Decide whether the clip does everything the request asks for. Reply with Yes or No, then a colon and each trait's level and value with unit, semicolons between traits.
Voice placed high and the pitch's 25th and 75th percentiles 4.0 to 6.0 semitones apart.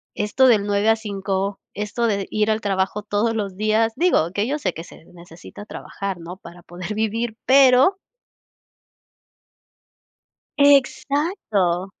No: high, 210 Hz; average, 3.3 semitones